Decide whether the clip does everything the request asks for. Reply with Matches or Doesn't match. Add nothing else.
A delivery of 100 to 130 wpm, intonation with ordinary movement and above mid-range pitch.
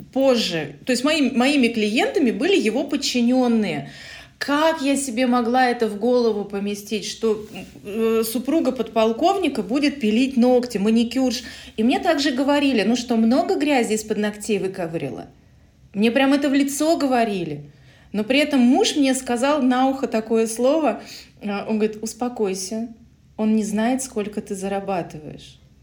Doesn't match